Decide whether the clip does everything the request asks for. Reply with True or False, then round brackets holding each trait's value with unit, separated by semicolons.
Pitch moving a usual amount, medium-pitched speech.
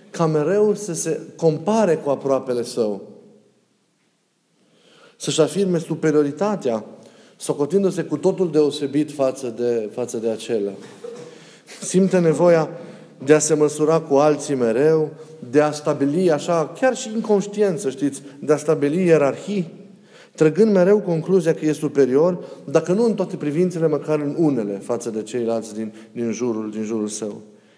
True (4.8 semitones; 155 Hz)